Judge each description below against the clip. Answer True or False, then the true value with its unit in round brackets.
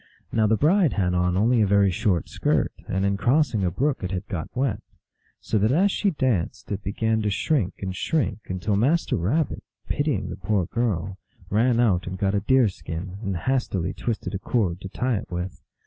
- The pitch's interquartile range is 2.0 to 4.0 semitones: False (4.9 semitones)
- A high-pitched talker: False (100 Hz)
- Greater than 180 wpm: True (200 wpm)